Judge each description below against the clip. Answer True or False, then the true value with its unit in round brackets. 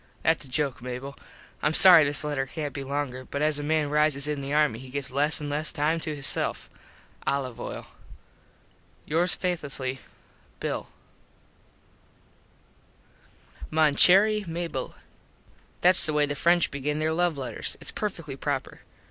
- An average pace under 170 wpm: True (150 wpm)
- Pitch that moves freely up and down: False (2.5 semitones)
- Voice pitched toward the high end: False (150 Hz)